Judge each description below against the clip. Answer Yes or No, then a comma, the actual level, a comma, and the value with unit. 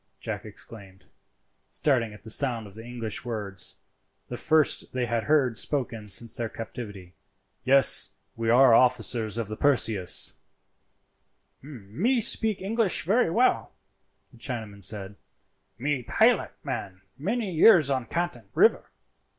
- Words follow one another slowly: Yes, slow, 130 wpm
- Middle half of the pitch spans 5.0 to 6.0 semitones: Yes, average, 5.3 semitones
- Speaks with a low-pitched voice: Yes, low, 120 Hz